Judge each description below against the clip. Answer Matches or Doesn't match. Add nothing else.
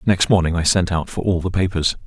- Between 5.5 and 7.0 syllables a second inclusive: Matches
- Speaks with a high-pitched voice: Doesn't match